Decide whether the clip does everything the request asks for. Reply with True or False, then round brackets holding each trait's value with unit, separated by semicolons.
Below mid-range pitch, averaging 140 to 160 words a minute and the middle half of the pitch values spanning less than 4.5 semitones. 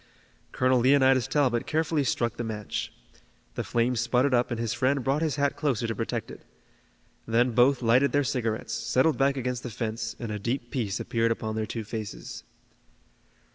False (120 Hz; 175 wpm; 2.9 semitones)